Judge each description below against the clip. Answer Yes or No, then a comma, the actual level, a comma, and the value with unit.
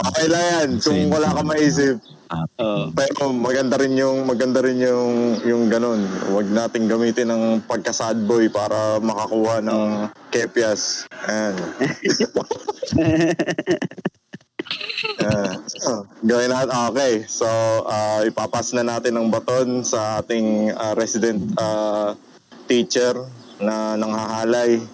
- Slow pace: Yes, slow, 105 wpm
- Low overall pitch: Yes, low, 115 Hz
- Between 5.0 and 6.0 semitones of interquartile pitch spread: No, average, 2.8 semitones